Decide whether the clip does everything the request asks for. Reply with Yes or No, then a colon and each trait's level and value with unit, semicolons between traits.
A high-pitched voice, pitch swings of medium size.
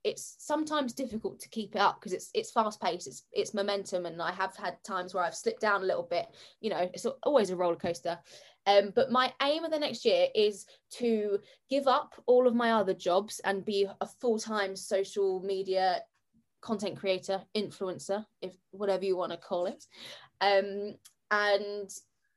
Yes: high, 200 Hz; average, 3.9 semitones